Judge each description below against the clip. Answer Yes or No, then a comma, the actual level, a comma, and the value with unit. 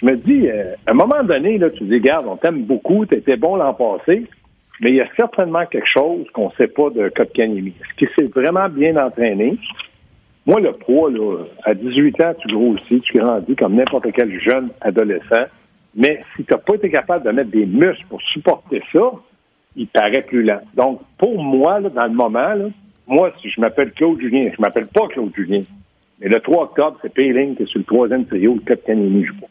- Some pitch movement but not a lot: No, wide, 7.4 semitones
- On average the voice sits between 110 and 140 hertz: Yes, low, 135 Hz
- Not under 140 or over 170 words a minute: No, fast, 220 wpm